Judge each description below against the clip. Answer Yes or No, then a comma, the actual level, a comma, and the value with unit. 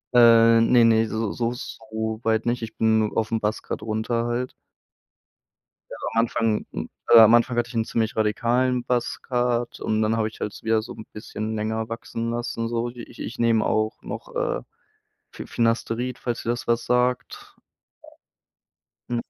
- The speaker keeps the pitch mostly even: Yes, narrow, 1.4 semitones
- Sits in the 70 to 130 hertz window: Yes, low, 115 Hz